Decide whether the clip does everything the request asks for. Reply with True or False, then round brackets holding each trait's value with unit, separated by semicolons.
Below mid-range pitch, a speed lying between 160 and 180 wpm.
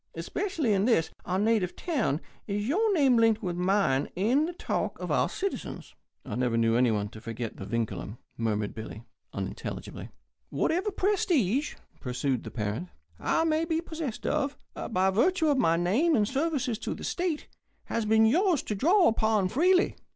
False (220 Hz; 165 wpm)